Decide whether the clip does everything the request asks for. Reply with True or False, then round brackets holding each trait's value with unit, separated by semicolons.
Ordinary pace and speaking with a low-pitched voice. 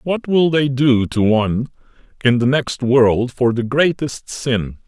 True (170 wpm; 130 Hz)